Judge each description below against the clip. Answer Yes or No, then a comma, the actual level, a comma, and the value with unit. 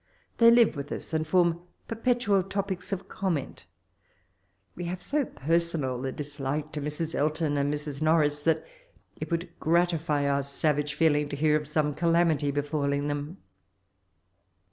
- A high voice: No, medium, 155 Hz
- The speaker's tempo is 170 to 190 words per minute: No, average, 145 wpm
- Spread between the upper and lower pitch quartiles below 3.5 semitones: Yes, average, 2.9 semitones